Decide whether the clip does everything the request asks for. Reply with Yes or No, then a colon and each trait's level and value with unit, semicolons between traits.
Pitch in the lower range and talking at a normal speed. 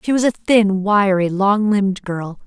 No: high, 200 Hz; average, 195 wpm